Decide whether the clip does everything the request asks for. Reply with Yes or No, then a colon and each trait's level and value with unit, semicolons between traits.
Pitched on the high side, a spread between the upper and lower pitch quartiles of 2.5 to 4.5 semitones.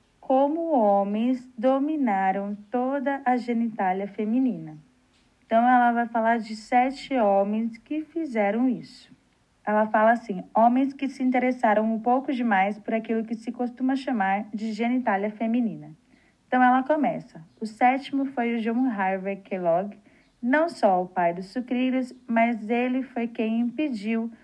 Yes: high, 235 Hz; average, 3.3 semitones